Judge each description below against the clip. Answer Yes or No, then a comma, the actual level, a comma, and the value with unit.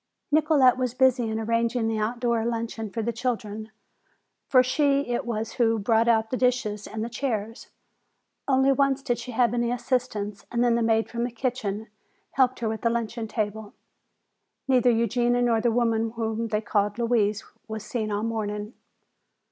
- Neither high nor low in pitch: No, high, 230 Hz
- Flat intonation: Yes, narrow, 2.0 semitones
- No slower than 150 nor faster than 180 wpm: Yes, average, 170 wpm